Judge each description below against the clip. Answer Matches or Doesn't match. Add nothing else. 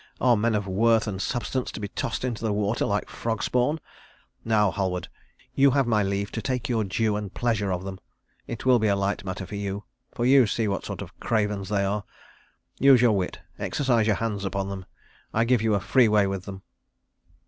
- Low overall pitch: Matches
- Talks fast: Matches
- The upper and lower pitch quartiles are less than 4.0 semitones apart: Matches